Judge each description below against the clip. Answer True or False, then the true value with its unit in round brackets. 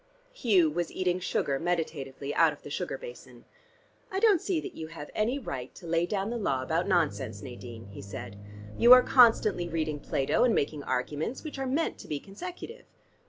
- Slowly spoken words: False (190 wpm)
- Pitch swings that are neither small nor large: False (9.0 semitones)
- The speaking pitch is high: False (170 Hz)